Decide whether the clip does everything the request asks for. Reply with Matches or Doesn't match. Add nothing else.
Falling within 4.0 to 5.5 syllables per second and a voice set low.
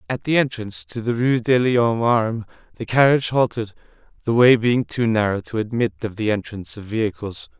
Doesn't match